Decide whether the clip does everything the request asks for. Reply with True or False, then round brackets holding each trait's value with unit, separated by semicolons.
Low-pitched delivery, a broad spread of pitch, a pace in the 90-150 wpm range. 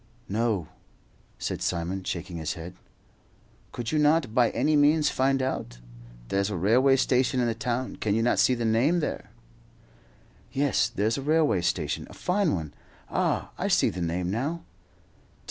False (115 Hz; 6.9 semitones; 165 wpm)